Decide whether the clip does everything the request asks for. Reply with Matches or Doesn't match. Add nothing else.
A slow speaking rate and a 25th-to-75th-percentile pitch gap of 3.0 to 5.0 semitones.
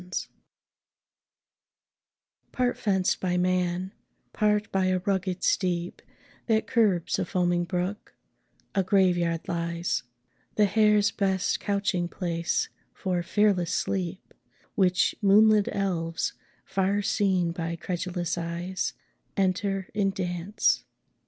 Doesn't match